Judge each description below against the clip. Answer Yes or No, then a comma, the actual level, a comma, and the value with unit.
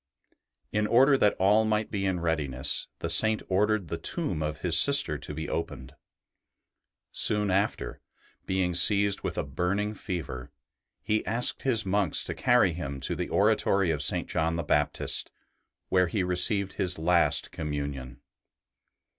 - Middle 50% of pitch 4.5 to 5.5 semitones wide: Yes, average, 4.8 semitones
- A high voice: No, very low, 90 Hz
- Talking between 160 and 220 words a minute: No, average, 150 wpm